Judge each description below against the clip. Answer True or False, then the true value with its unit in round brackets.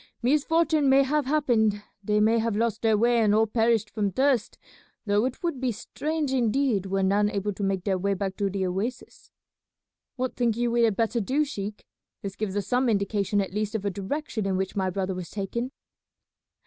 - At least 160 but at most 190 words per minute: False (200 wpm)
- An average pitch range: True (3.9 semitones)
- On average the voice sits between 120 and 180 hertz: False (215 Hz)